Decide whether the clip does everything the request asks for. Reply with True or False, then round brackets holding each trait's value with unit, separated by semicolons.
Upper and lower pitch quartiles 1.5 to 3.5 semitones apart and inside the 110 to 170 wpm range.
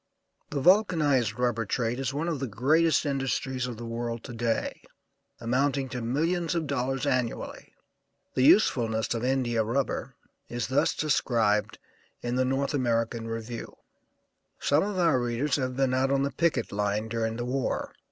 True (3.1 semitones; 160 wpm)